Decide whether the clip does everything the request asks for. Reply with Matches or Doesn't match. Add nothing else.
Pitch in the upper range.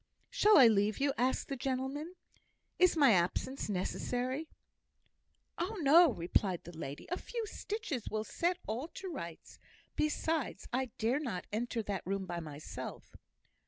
Matches